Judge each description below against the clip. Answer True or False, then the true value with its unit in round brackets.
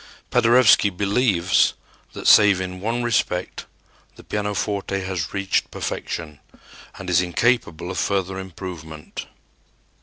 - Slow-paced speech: True (110 wpm)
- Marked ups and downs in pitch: False (2.6 semitones)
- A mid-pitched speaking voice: False (95 Hz)